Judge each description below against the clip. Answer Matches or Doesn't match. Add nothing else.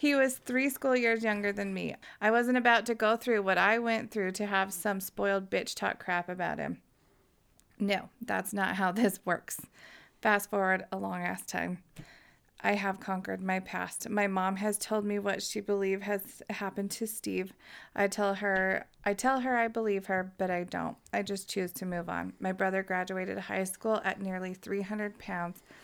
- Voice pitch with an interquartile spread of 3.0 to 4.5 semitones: Doesn't match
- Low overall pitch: Doesn't match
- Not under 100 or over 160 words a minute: Doesn't match